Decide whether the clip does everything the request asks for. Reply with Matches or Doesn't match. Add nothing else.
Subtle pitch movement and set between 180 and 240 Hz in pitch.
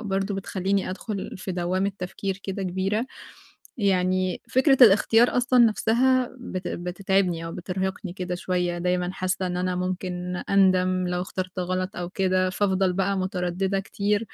Matches